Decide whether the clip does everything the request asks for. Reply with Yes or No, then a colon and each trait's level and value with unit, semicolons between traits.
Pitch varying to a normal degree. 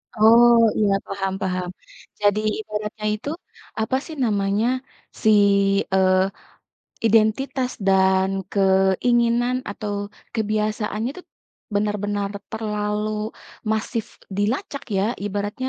No: narrow, 2.2 semitones